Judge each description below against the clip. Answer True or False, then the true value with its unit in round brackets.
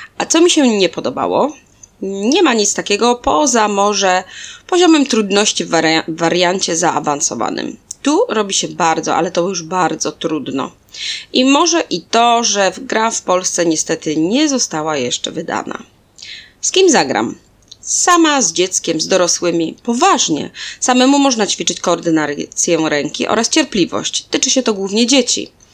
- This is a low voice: False (200 Hz)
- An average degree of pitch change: False (7.6 semitones)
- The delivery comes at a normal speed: True (140 wpm)